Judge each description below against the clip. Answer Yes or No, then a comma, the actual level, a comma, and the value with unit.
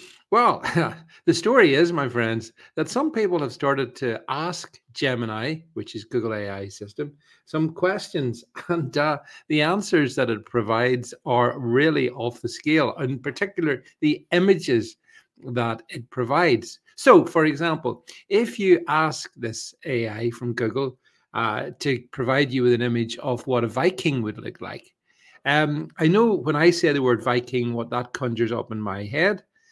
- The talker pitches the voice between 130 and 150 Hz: Yes, medium, 140 Hz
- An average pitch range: No, wide, 6.1 semitones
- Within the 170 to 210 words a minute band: No, average, 160 wpm